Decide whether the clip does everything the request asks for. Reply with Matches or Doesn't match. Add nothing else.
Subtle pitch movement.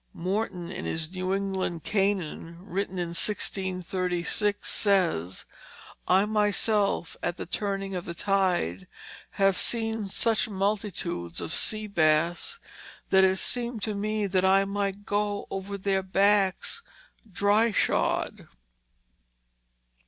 Matches